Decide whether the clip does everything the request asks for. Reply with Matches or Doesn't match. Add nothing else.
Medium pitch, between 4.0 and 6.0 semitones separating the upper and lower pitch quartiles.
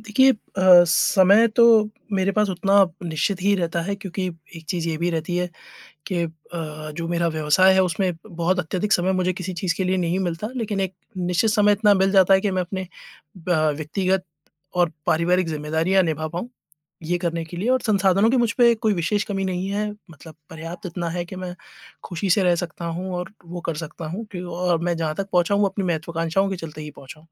Doesn't match